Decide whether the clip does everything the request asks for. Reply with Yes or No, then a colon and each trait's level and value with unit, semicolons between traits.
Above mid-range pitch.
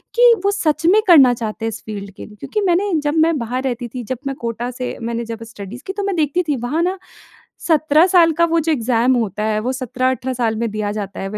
Yes: very high, 255 Hz